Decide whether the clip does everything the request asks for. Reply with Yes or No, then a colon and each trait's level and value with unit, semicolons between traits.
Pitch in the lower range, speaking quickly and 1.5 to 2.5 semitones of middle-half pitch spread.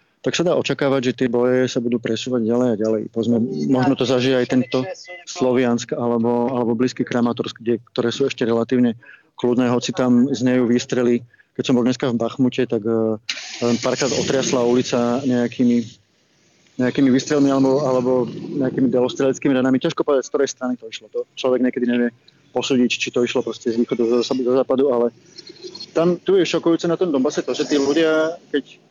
Yes: low, 125 Hz; fast, 180 wpm; narrow, 2.1 semitones